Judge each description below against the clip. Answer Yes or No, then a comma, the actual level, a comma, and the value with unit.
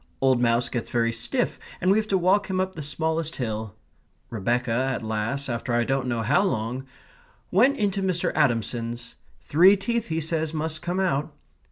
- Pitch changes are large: Yes, wide, 7.5 semitones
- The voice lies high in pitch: No, medium, 145 Hz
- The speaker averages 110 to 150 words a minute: No, average, 180 wpm